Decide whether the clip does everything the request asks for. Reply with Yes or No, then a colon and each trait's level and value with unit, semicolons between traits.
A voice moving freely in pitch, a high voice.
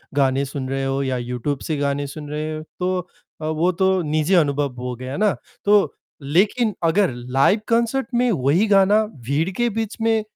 No: wide, 6.8 semitones; medium, 155 Hz